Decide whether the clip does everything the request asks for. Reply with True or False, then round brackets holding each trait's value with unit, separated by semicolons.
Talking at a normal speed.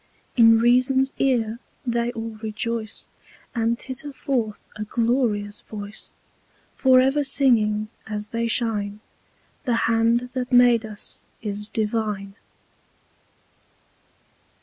False (105 wpm)